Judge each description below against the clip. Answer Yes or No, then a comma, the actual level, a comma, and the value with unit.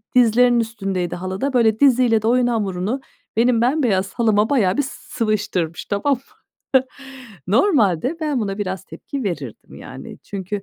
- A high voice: Yes, high, 220 Hz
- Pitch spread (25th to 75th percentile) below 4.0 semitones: No, average, 4.3 semitones